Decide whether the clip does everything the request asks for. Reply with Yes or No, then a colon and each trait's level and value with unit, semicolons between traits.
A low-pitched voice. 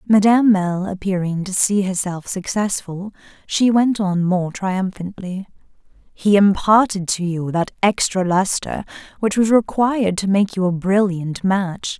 No: high, 195 Hz